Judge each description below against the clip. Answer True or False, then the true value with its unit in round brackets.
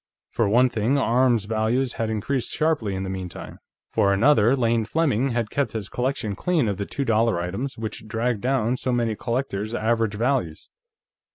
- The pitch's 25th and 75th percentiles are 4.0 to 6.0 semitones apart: False (3.5 semitones)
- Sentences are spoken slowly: False (175 wpm)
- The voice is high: False (115 Hz)